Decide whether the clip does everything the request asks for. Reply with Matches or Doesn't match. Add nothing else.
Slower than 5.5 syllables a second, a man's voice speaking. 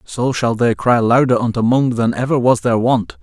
Matches